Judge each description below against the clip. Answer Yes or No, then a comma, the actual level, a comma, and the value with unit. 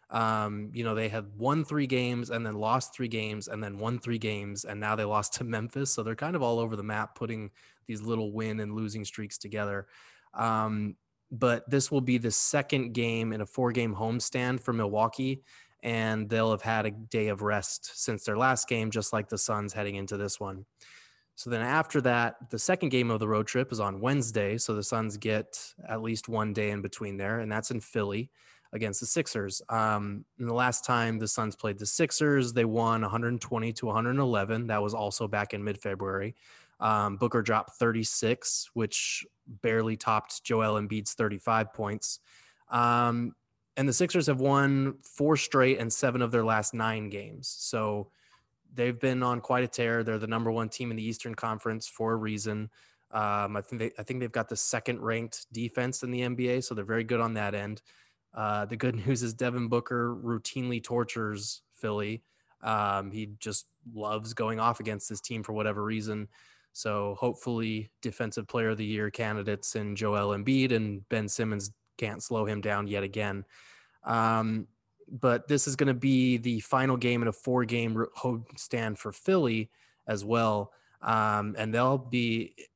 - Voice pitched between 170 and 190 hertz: No, low, 115 Hz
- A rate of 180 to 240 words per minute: Yes, average, 190 wpm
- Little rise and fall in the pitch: Yes, narrow, 2.2 semitones